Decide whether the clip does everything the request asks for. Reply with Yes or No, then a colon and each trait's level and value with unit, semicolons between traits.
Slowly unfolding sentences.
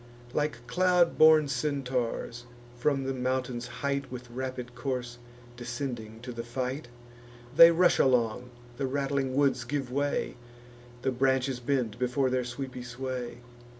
Yes: slow, 130 wpm